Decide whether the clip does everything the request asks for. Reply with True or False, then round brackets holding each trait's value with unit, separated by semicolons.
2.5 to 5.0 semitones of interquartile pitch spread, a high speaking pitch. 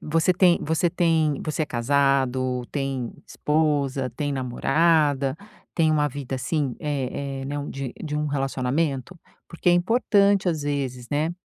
False (3.2 semitones; 145 Hz)